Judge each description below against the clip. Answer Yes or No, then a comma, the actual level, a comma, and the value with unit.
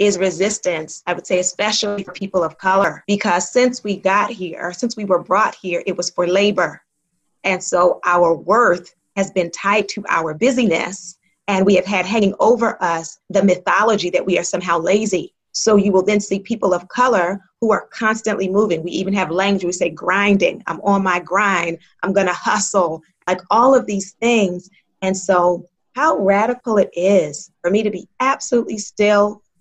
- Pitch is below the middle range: No, high, 190 Hz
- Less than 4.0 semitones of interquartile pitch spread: Yes, narrow, 2.6 semitones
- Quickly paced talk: No, average, 185 wpm